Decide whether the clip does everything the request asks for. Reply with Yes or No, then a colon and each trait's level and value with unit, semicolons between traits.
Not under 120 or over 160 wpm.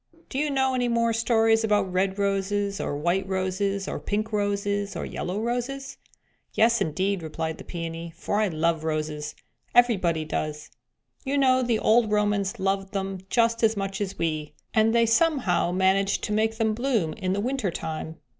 No: average, 175 wpm